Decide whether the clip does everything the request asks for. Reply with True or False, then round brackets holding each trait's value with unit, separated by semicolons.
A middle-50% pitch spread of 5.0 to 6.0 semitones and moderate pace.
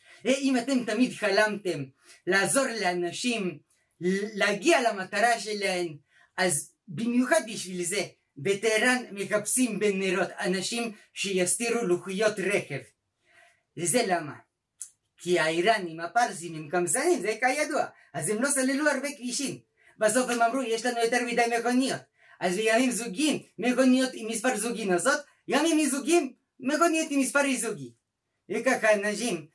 True (5.5 semitones; 120 wpm)